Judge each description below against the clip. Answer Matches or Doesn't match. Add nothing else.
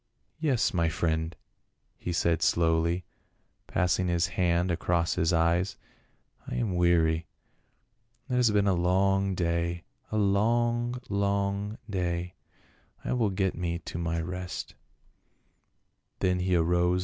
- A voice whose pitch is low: Matches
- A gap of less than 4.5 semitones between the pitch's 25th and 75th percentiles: Matches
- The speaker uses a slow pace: Matches